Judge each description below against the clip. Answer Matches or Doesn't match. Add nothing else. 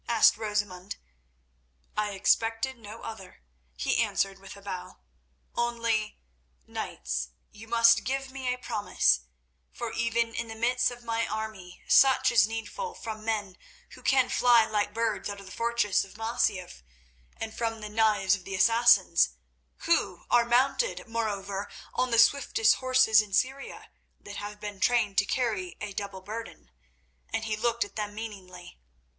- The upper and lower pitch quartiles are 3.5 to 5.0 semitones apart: Doesn't match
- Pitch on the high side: Matches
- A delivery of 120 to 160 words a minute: Matches